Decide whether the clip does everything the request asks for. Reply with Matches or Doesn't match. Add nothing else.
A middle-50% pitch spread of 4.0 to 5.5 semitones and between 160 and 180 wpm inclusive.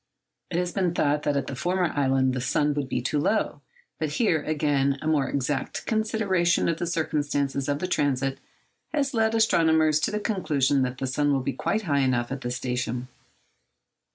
Doesn't match